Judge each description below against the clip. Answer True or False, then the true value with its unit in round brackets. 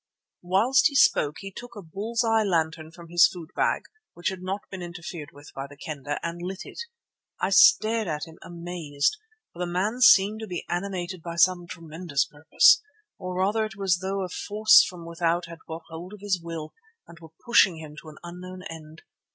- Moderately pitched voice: True (175 Hz)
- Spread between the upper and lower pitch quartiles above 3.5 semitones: False (3.1 semitones)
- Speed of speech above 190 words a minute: True (200 wpm)